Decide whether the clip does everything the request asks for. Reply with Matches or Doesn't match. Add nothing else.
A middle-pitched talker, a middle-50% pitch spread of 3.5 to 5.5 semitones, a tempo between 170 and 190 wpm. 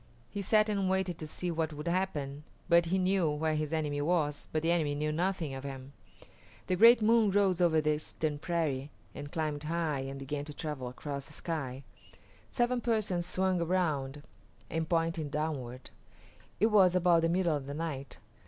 Matches